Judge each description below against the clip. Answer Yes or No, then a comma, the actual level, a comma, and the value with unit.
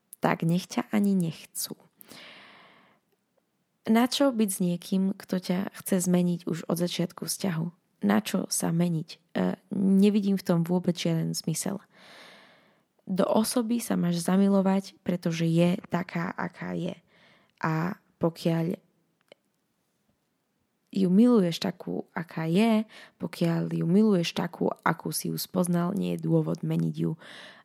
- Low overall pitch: No, medium, 185 Hz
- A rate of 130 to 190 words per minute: No, average, 120 wpm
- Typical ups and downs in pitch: Yes, average, 3.0 semitones